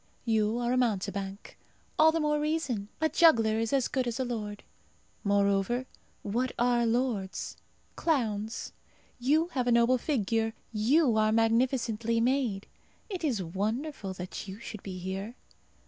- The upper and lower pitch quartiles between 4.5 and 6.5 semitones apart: No, average, 3.7 semitones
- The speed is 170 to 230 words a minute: No, average, 145 wpm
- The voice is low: No, high, 230 Hz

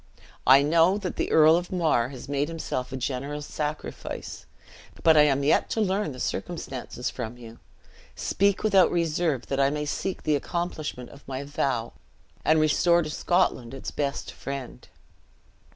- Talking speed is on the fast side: No, average, 160 wpm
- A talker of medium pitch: Yes, medium, 150 Hz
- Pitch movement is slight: No, average, 4.0 semitones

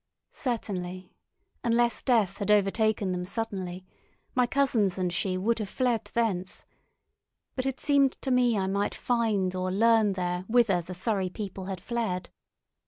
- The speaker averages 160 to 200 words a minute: No, average, 150 wpm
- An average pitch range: Yes, average, 4.1 semitones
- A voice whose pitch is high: Yes, high, 205 Hz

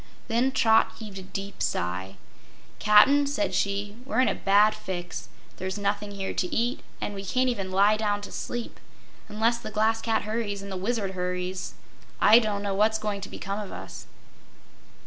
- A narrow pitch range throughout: Yes, narrow, 2.3 semitones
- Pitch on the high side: Yes, high, 205 Hz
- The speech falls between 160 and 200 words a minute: Yes, average, 180 wpm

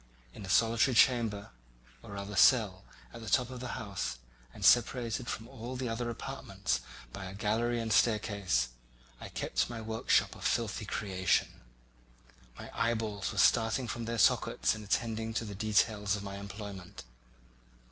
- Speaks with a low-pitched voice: Yes, low, 110 Hz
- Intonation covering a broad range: No, average, 2.7 semitones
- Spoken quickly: No, average, 155 wpm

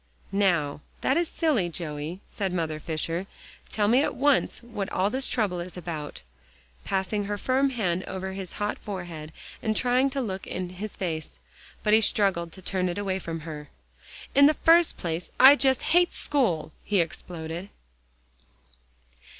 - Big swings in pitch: Yes, wide, 5.7 semitones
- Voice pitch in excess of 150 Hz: Yes, high, 190 Hz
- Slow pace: No, average, 160 wpm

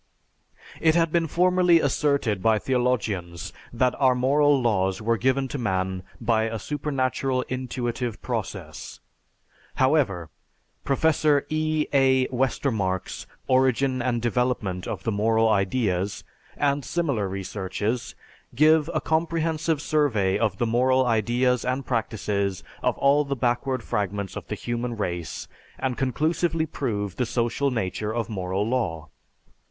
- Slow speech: Yes, slow, 125 wpm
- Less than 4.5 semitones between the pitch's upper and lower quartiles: No, average, 4.9 semitones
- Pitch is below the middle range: Yes, low, 125 Hz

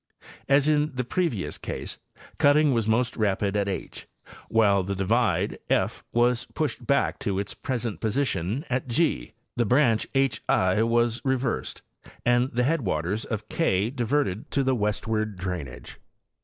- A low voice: Yes, low, 115 Hz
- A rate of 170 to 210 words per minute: No, average, 155 wpm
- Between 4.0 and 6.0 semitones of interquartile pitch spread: Yes, average, 4.7 semitones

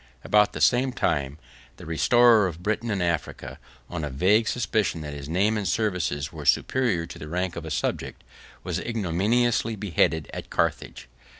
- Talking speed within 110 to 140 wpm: No, average, 170 wpm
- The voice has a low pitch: Yes, very low, 90 Hz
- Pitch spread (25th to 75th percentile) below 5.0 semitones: No, wide, 5.6 semitones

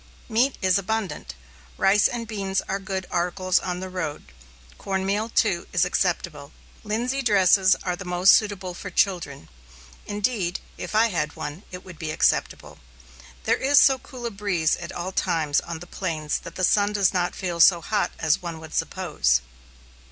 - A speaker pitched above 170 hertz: Yes, medium, 185 Hz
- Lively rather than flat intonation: No, average, 3.2 semitones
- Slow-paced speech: No, average, 170 wpm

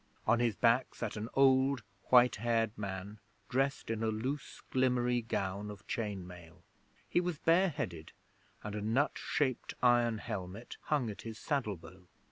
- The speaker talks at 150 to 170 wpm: Yes, average, 160 wpm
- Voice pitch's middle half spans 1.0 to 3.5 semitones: No, average, 4.3 semitones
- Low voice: Yes, low, 115 Hz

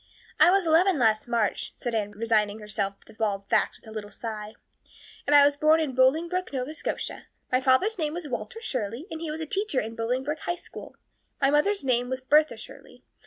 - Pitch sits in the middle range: No, very high, 260 Hz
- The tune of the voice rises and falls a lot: Yes, wide, 6.1 semitones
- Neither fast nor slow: No, fast, 210 wpm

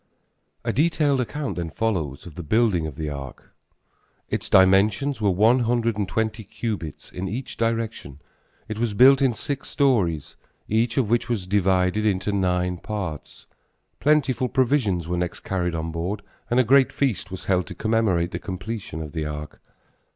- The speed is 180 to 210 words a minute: No, average, 165 wpm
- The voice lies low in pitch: Yes, low, 105 Hz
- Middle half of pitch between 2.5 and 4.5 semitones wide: No, average, 5.1 semitones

